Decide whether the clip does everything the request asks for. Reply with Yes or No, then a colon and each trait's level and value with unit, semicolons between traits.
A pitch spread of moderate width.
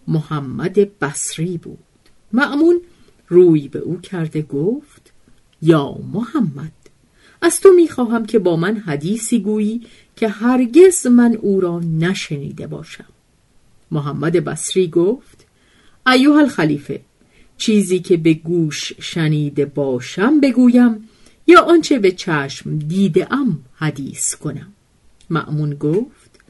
No: wide, 7.6 semitones